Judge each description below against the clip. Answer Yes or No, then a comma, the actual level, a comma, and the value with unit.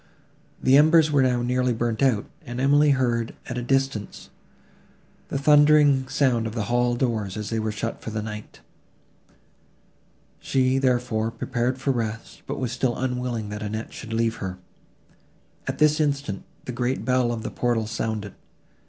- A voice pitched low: Yes, low, 120 Hz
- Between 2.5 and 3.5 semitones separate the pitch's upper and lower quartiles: Yes, average, 2.9 semitones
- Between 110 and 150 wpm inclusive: No, average, 160 wpm